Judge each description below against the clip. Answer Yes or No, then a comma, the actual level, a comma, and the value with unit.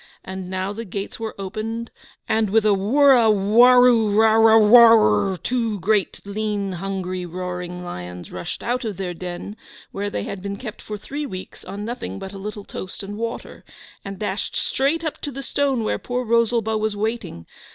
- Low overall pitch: No, high, 210 Hz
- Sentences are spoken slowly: No, average, 165 wpm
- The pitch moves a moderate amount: Yes, average, 3.3 semitones